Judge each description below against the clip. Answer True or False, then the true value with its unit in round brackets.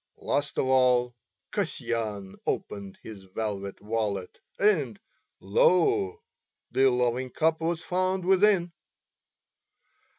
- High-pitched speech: False (125 Hz)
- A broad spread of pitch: True (8.8 semitones)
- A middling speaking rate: False (95 wpm)